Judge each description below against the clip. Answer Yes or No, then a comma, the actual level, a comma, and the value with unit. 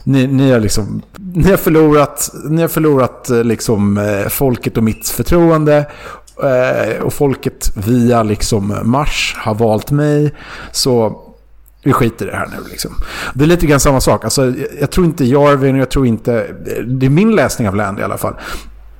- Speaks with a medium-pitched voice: No, low, 130 Hz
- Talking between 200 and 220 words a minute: No, average, 165 wpm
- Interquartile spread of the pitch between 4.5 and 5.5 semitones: Yes, average, 4.8 semitones